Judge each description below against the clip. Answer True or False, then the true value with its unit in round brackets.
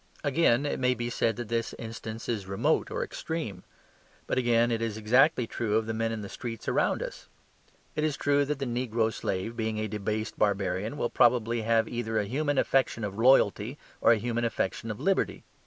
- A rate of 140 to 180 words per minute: False (200 wpm)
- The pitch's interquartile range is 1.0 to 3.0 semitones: True (2.5 semitones)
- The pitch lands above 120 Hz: False (115 Hz)